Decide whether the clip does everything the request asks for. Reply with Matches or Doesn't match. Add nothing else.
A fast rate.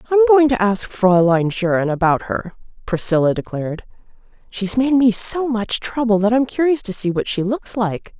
Doesn't match